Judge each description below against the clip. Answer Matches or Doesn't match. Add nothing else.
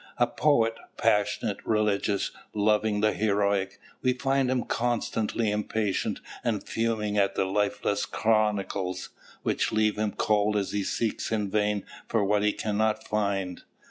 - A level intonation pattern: Matches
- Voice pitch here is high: Doesn't match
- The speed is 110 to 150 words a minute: Matches